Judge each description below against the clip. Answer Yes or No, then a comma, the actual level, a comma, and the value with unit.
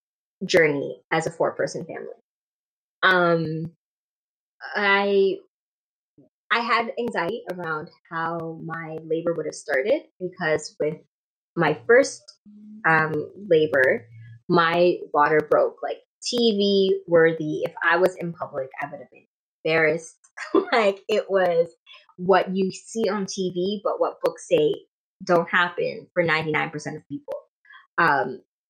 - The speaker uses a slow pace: Yes, slow, 125 wpm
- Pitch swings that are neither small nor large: Yes, average, 4.4 semitones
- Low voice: No, medium, 180 Hz